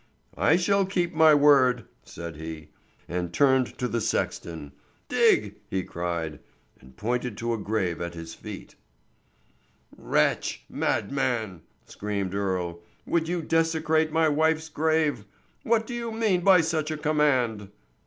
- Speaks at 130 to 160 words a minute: Yes, slow, 135 wpm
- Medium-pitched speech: No, low, 130 Hz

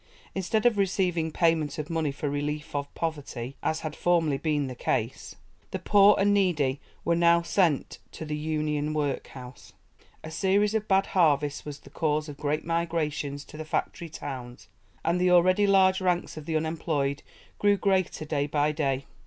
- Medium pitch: Yes, medium, 160 Hz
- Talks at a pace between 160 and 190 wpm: Yes, average, 170 wpm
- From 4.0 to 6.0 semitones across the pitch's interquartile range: No, average, 3.5 semitones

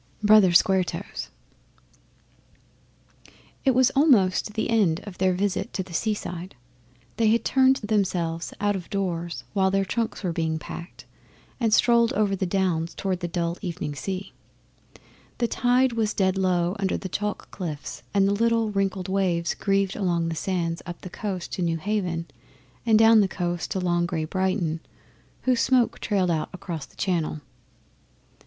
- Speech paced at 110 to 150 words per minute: No, average, 160 wpm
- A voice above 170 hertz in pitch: Yes, high, 190 Hz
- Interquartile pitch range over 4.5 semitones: No, average, 3.5 semitones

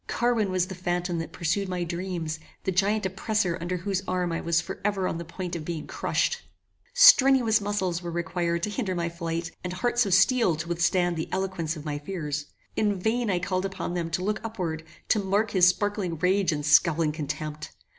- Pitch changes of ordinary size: Yes, average, 3.0 semitones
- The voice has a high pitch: No, medium, 180 Hz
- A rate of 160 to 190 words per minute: No, average, 200 wpm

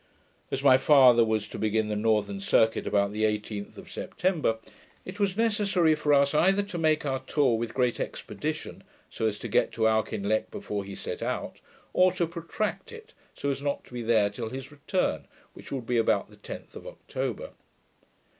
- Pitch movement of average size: No, wide, 7.1 semitones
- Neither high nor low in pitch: No, low, 130 Hz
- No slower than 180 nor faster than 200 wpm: Yes, average, 185 wpm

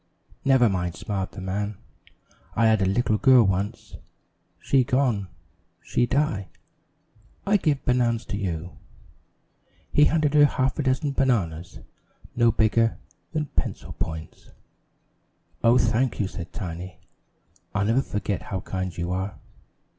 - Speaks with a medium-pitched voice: No, low, 110 Hz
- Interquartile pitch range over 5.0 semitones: Yes, wide, 5.4 semitones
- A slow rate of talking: Yes, slow, 125 wpm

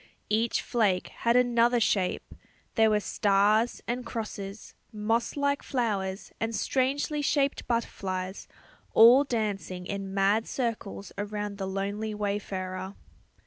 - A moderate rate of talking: No, slow, 115 wpm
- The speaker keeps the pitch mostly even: No, average, 3.2 semitones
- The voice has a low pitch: No, high, 215 Hz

